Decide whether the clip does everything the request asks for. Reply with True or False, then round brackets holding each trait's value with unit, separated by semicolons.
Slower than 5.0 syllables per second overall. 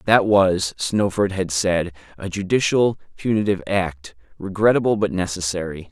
True (4.7 syllables/s)